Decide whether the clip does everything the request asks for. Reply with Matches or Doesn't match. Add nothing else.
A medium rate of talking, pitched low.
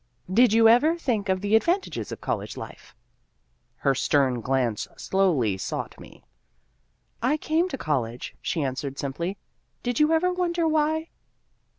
Doesn't match